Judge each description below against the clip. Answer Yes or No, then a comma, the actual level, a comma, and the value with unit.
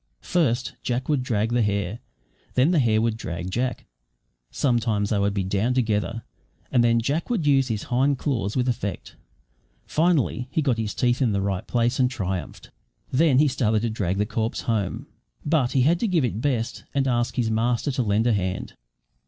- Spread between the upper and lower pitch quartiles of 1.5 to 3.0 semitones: No, average, 3.7 semitones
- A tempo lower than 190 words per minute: No, average, 195 wpm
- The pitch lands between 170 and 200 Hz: No, low, 120 Hz